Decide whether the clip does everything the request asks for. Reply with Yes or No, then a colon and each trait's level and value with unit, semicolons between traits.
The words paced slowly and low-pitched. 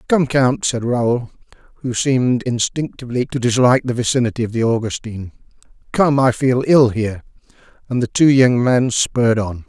No: average, 160 wpm; low, 125 Hz